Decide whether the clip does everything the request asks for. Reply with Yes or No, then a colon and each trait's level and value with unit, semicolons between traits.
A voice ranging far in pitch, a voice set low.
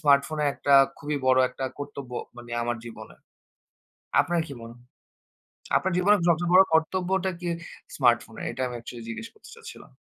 No: wide, 6.4 semitones; medium, 145 Hz